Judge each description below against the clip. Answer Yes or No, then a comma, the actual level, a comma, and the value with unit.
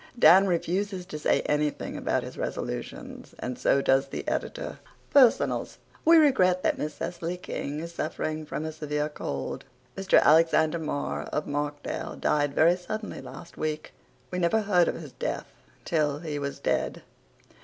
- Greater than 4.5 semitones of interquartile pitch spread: No, average, 3.4 semitones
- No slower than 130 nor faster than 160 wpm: Yes, average, 155 wpm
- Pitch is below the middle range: No, medium, 160 Hz